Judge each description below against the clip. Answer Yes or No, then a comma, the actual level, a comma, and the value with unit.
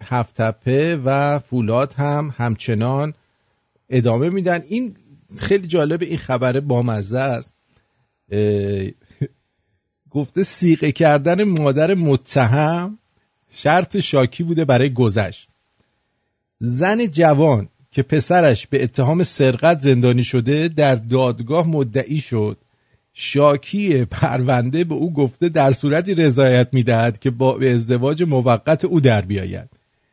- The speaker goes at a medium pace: No, slow, 110 wpm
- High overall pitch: No, low, 135 Hz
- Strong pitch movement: No, average, 4.8 semitones